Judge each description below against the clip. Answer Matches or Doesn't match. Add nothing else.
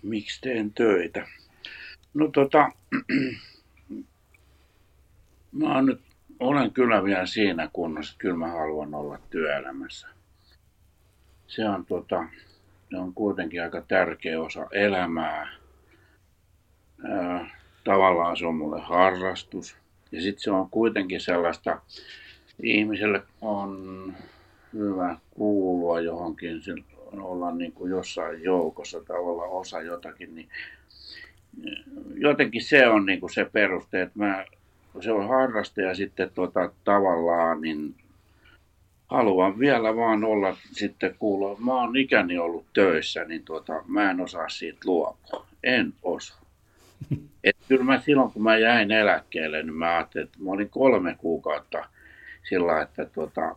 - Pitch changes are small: Doesn't match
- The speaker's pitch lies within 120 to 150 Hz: Doesn't match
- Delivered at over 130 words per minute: Doesn't match